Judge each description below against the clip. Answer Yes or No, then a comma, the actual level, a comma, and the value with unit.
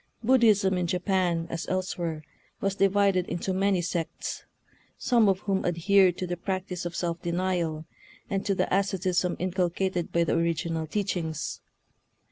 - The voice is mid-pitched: Yes, medium, 180 Hz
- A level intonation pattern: Yes, narrow, 2.3 semitones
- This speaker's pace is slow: No, average, 145 wpm